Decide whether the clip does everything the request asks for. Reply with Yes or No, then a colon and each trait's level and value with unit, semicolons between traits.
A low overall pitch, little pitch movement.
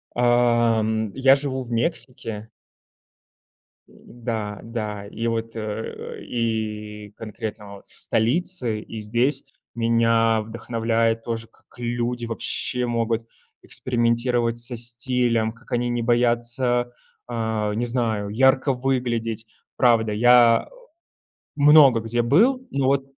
Yes: low, 115 Hz; narrow, 1.5 semitones